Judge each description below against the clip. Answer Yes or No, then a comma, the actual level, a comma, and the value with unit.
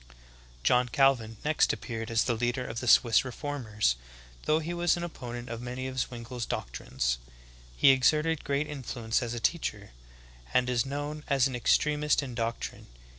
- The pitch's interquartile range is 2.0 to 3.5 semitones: No, average, 3.9 semitones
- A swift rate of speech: No, average, 170 wpm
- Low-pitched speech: Yes, low, 125 Hz